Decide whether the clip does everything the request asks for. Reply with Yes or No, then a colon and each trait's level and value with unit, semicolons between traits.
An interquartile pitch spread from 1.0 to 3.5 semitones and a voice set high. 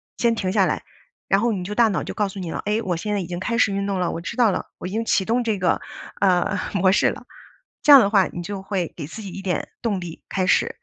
Yes: average, 2.9 semitones; high, 195 Hz